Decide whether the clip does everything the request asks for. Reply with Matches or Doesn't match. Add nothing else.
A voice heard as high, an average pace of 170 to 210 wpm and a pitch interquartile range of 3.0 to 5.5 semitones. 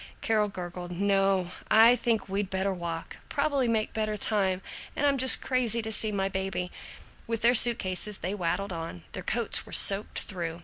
Matches